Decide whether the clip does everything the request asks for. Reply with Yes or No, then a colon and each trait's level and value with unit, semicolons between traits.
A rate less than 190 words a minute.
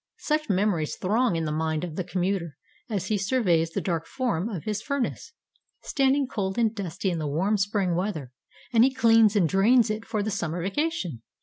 No: average, 195 wpm